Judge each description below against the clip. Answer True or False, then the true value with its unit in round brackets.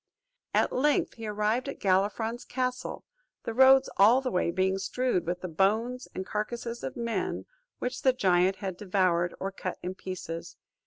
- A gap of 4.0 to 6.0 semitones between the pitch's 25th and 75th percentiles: True (5.0 semitones)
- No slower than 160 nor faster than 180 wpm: True (165 wpm)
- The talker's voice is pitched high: True (210 Hz)